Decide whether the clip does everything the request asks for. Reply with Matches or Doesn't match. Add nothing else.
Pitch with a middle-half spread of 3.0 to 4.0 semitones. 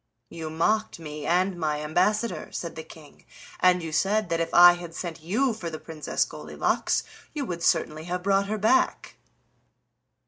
Matches